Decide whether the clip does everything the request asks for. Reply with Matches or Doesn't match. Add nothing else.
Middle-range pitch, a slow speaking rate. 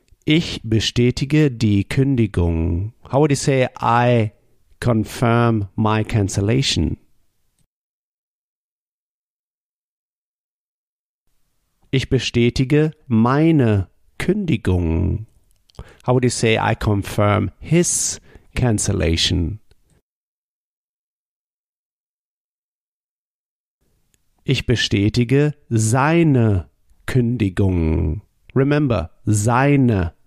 Doesn't match